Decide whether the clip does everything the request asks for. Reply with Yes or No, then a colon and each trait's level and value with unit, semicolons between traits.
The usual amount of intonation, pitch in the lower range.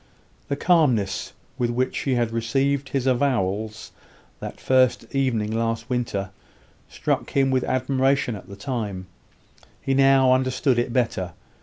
Yes: average, 3.2 semitones; low, 125 Hz